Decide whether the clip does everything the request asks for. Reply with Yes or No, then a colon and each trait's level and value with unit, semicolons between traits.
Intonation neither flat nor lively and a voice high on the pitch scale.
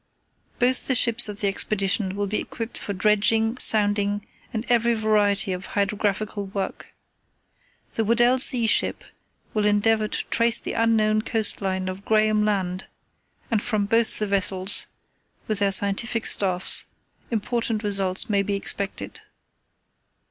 No: narrow, 2.0 semitones; high, 210 Hz